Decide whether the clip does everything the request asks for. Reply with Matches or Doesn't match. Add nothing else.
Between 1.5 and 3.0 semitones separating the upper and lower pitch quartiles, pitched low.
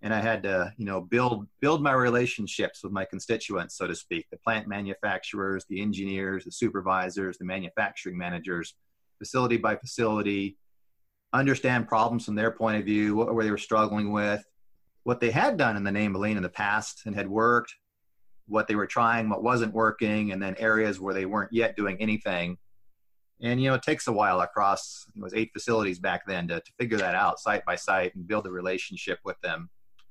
Matches